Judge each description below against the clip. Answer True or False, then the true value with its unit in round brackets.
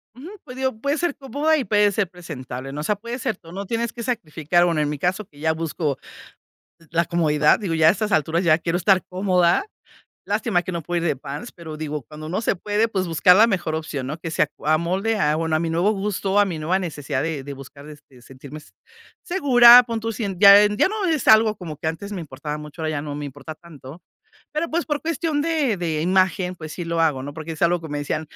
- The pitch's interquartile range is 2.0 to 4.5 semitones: False (5.6 semitones)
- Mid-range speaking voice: True (175 Hz)